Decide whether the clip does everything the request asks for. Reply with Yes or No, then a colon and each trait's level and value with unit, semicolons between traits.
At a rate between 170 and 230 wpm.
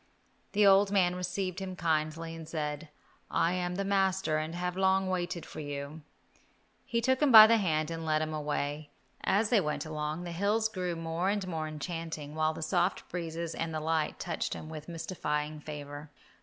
Yes: average, 185 wpm